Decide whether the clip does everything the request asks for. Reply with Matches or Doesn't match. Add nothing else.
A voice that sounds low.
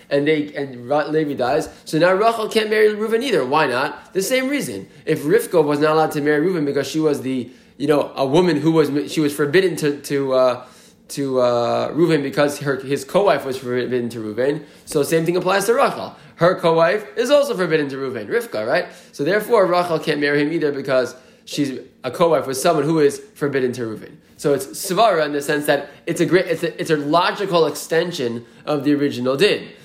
Doesn't match